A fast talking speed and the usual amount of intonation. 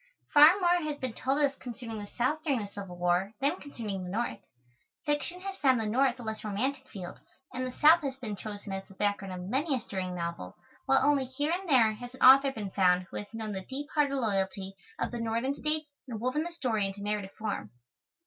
No: fast, 225 wpm; wide, 5.7 semitones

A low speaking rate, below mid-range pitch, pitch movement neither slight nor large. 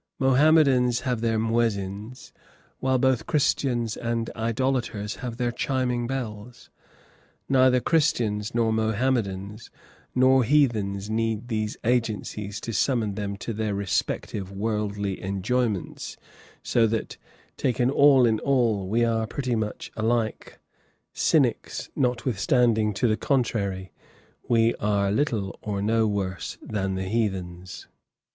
Yes: slow, 115 wpm; low, 115 Hz; average, 3.2 semitones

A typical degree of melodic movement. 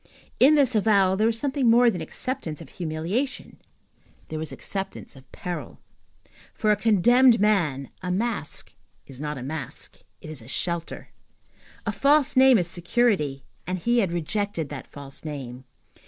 No: wide, 7.1 semitones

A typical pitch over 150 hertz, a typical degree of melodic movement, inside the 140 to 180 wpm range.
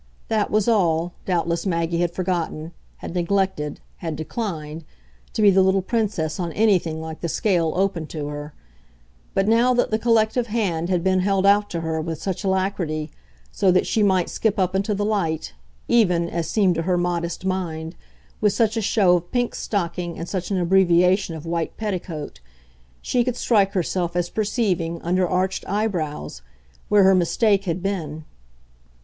Yes: medium, 185 Hz; average, 3.3 semitones; average, 170 wpm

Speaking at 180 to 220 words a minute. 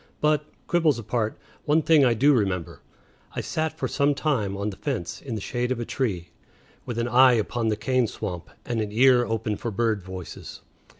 Yes: average, 195 wpm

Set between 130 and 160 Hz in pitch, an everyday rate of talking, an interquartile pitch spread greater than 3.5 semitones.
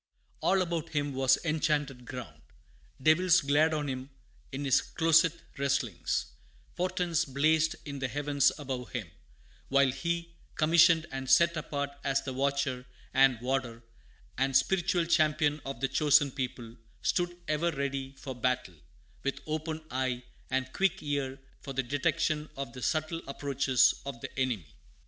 No: medium, 140 Hz; average, 145 wpm; average, 3.0 semitones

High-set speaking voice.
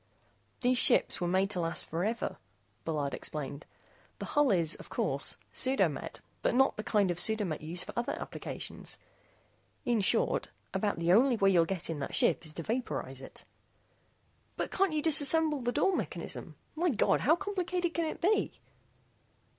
Yes: high, 215 Hz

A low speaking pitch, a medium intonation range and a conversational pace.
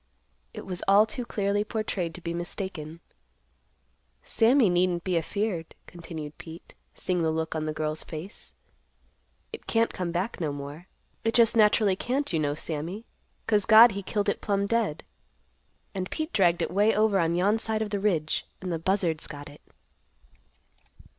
No: medium, 185 Hz; average, 4.5 semitones; average, 165 wpm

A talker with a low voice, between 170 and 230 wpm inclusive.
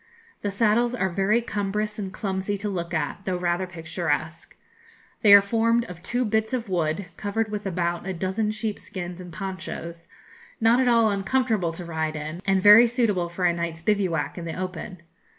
No: high, 190 Hz; average, 180 wpm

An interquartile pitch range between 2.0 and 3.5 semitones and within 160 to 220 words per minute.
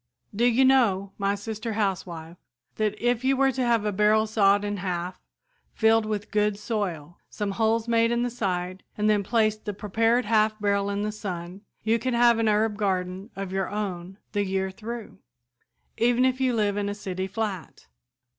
Yes: narrow, 2.6 semitones; average, 185 wpm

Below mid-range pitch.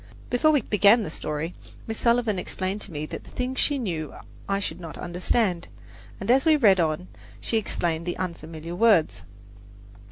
No: high, 190 Hz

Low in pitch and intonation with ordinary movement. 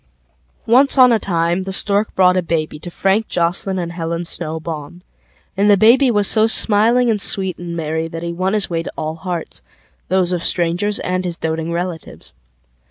No: medium, 180 Hz; average, 3.5 semitones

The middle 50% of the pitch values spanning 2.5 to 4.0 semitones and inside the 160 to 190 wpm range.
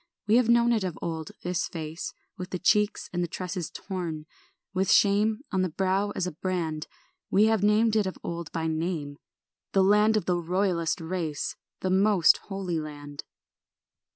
Yes: average, 3.7 semitones; average, 175 wpm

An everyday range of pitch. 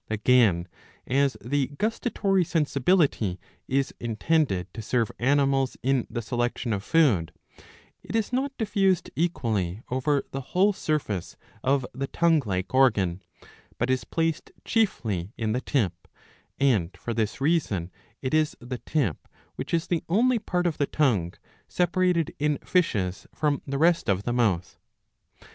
No: wide, 7.0 semitones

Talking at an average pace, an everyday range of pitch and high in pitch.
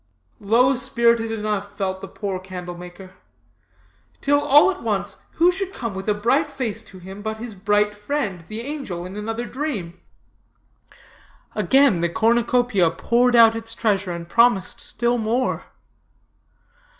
Yes: average, 145 wpm; average, 4.1 semitones; high, 220 Hz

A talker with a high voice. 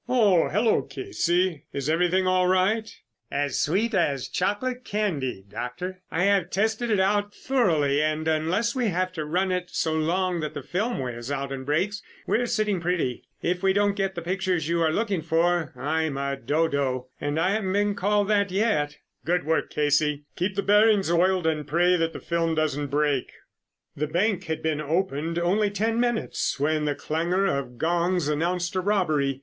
No: medium, 175 Hz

